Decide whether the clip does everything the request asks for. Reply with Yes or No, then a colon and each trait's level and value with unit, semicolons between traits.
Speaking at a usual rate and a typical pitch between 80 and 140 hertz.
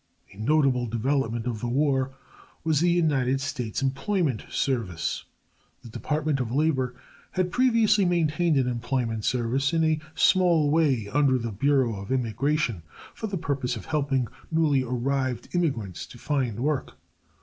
Yes: average, 145 wpm; low, 135 Hz